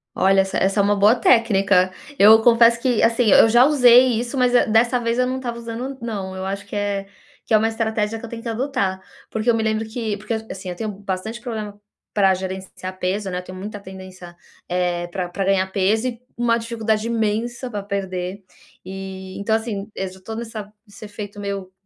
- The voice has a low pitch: No, high, 210 Hz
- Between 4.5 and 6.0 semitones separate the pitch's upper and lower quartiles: No, average, 3.3 semitones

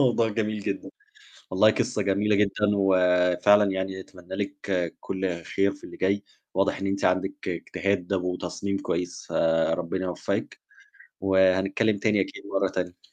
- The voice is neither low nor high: No, very low, 95 Hz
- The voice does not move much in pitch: Yes, narrow, 1.8 semitones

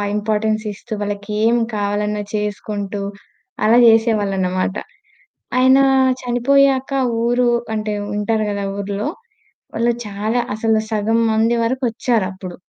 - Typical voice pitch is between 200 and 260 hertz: Yes, high, 215 Hz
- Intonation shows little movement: Yes, narrow, 2.3 semitones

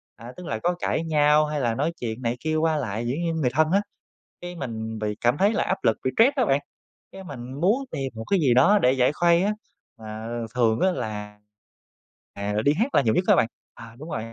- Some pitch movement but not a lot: No, wide, 6.9 semitones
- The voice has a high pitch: No, low, 135 Hz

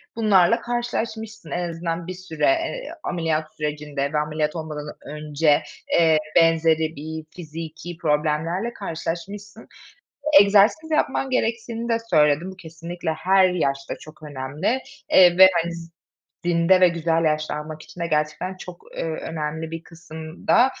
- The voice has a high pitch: No, medium, 165 Hz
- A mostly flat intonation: No, average, 3.4 semitones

